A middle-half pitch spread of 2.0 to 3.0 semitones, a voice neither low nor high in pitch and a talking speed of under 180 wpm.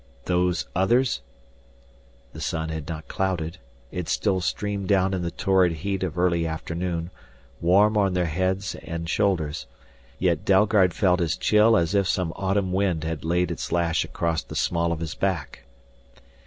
No: narrow, 2.6 semitones; very low, 90 Hz; average, 160 wpm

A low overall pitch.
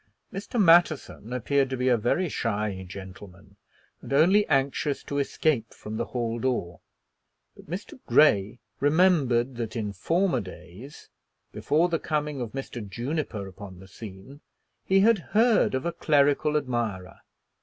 Yes: low, 130 Hz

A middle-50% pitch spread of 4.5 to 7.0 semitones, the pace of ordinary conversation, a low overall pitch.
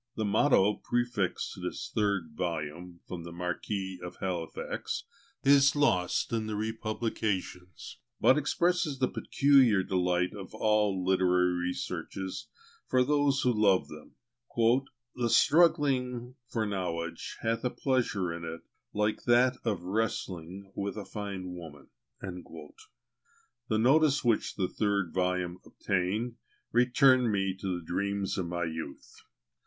No: average, 5.2 semitones; slow, 125 wpm; low, 100 Hz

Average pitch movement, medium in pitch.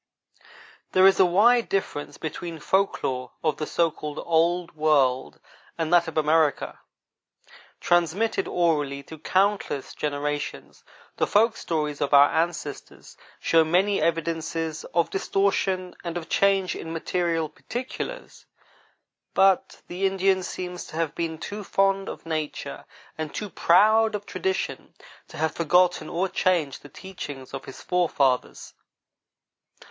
Yes: average, 3.7 semitones; medium, 170 Hz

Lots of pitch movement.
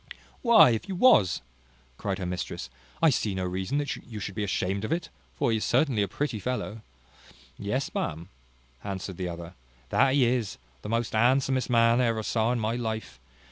No: average, 4.7 semitones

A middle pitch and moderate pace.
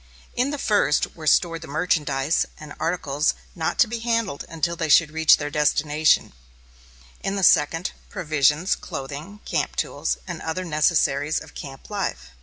Yes: medium, 160 Hz; average, 155 wpm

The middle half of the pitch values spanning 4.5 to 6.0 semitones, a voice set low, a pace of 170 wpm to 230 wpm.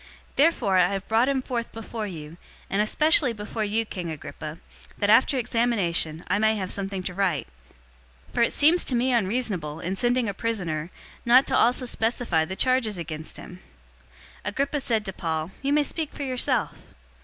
No: wide, 5.4 semitones; high, 215 Hz; average, 180 wpm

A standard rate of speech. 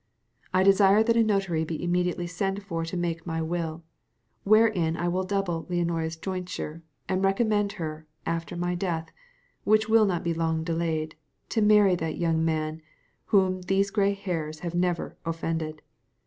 Yes: average, 160 wpm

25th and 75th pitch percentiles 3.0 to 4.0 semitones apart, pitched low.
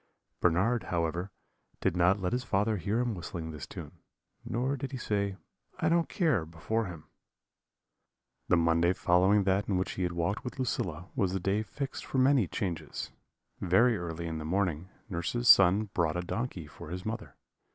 No: average, 4.7 semitones; very low, 95 Hz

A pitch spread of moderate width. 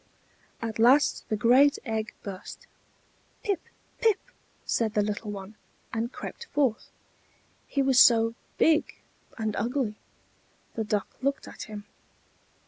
Yes: average, 4.3 semitones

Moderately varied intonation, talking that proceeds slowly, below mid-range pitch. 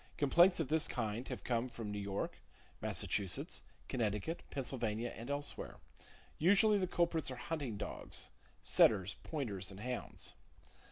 No: wide, 7.1 semitones; slow, 125 wpm; low, 125 Hz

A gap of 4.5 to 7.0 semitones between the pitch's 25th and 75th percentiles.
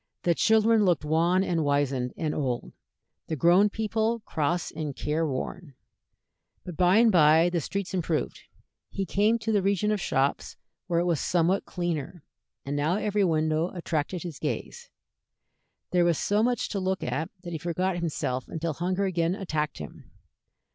No: average, 3.9 semitones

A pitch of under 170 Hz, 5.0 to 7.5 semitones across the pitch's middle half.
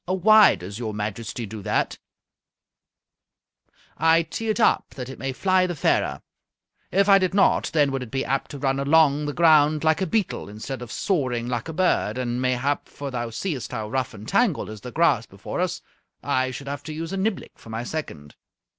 Yes: low, 135 Hz; wide, 5.5 semitones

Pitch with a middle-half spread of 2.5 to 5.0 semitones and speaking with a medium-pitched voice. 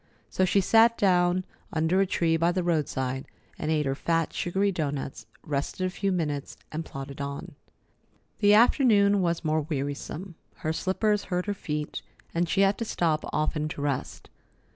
Yes: average, 4.3 semitones; medium, 170 Hz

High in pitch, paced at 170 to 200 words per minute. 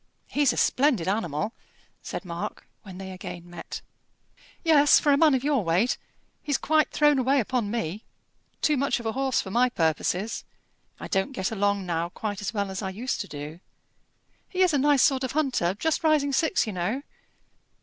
Yes: high, 225 Hz; average, 185 wpm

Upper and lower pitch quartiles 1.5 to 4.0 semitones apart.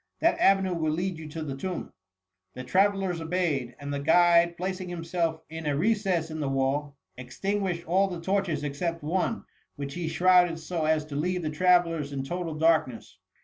Yes: average, 3.3 semitones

